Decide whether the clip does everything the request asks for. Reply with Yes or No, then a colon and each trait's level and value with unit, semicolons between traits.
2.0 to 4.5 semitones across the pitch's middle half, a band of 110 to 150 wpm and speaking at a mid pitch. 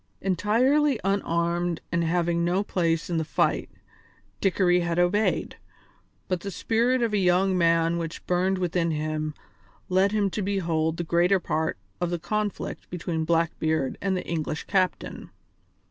Yes: average, 2.7 semitones; average, 145 wpm; medium, 175 Hz